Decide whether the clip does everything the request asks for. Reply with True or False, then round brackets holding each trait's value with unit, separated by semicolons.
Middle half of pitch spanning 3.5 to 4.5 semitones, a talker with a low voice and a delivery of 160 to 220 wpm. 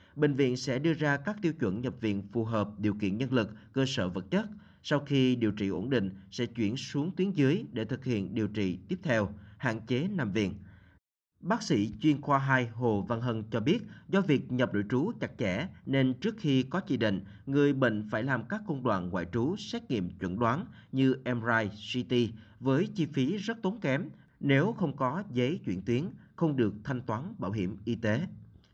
False (5.0 semitones; 125 Hz; 210 wpm)